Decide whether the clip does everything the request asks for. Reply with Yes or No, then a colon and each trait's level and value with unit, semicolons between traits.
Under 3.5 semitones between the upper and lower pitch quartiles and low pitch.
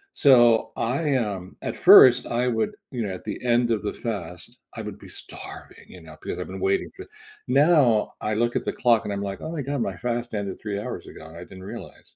No: average, 4.1 semitones; low, 110 Hz